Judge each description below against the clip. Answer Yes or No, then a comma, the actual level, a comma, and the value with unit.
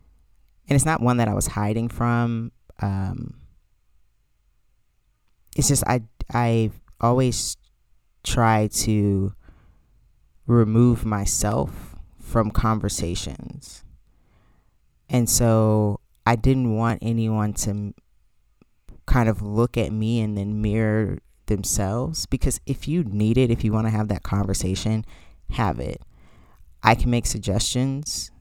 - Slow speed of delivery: Yes, slow, 120 wpm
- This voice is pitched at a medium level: No, low, 110 Hz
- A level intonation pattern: No, average, 3.5 semitones